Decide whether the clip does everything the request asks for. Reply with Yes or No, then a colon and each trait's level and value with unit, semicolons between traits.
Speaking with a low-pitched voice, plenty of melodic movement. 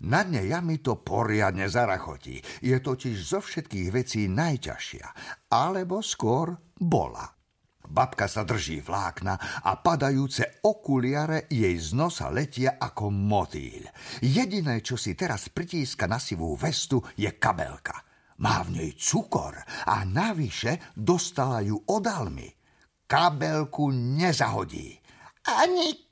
Yes: low, 130 Hz; wide, 7.4 semitones